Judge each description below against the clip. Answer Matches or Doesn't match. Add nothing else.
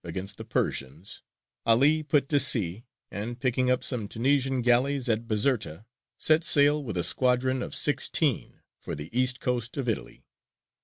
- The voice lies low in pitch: Matches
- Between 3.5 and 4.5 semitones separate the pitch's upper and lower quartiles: Matches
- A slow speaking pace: Doesn't match